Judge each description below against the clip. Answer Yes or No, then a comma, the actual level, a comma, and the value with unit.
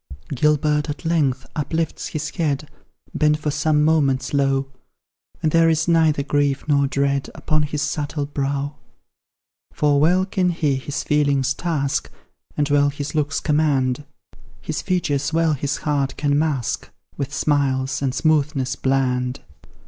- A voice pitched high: No, medium, 145 Hz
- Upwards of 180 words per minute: No, average, 140 wpm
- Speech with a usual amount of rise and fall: No, narrow, 1.9 semitones